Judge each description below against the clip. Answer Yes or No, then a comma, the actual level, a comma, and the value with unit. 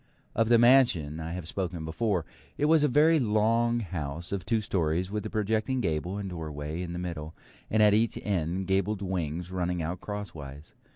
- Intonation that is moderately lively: Yes, average, 4.8 semitones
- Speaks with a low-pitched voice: Yes, very low, 95 Hz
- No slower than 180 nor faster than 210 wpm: Yes, average, 185 wpm